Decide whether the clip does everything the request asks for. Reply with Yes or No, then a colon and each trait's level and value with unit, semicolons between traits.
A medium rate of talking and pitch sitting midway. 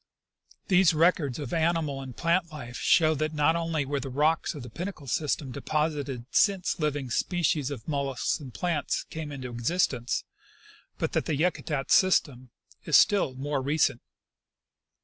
Yes: average, 155 wpm; medium, 150 Hz